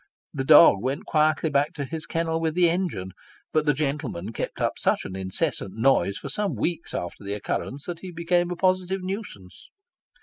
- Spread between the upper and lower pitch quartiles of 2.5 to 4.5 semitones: No, average, 5.1 semitones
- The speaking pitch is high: No, medium, 155 Hz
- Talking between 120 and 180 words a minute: No, average, 190 wpm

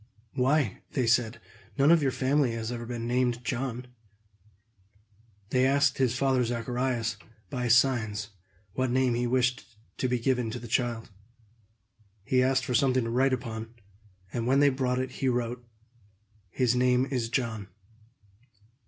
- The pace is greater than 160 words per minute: No, average, 150 wpm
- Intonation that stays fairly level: Yes, narrow, 1.9 semitones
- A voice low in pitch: Yes, low, 125 Hz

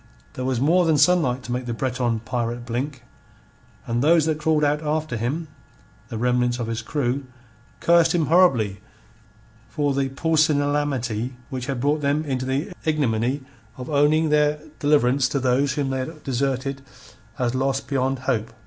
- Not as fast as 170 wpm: Yes, average, 160 wpm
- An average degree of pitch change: Yes, average, 3.3 semitones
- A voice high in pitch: No, low, 135 Hz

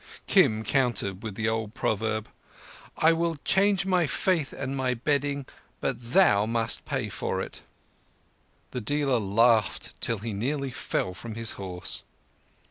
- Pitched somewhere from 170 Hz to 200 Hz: No, low, 120 Hz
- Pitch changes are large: No, average, 4.6 semitones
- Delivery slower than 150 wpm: Yes, average, 140 wpm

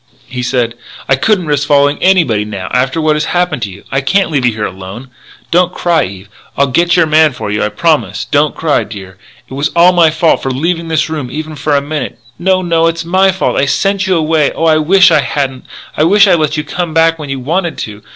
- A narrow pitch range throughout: No, average, 4.4 semitones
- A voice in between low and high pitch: Yes, medium, 155 Hz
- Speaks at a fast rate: Yes, fast, 250 wpm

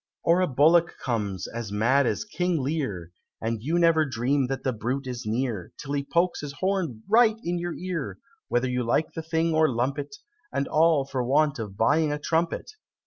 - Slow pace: No, average, 195 wpm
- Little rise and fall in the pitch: No, average, 5.2 semitones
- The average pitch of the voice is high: No, medium, 140 Hz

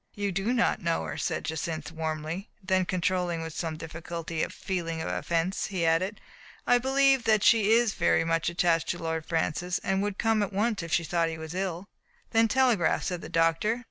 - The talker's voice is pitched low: No, medium, 175 Hz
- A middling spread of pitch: Yes, average, 3.9 semitones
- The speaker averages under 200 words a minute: No, fast, 205 wpm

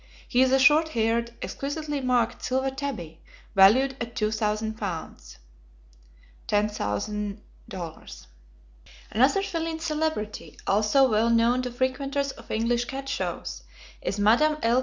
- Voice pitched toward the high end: Yes, high, 240 Hz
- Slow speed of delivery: Yes, slow, 120 wpm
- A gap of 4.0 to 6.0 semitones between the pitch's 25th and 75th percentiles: Yes, average, 4.4 semitones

